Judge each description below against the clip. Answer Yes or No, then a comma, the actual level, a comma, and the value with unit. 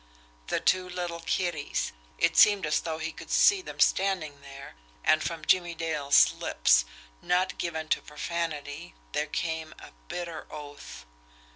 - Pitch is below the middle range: No, medium, 160 Hz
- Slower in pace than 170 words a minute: Yes, average, 145 wpm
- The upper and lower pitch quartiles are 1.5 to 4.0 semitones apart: Yes, average, 3.1 semitones